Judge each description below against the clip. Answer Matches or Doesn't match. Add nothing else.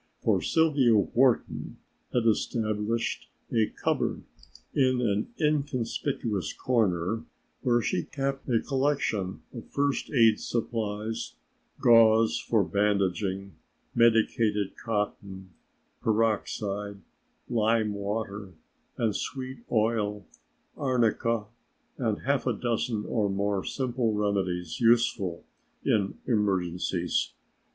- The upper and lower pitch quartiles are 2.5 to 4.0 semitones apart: Matches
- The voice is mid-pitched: Doesn't match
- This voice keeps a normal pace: Doesn't match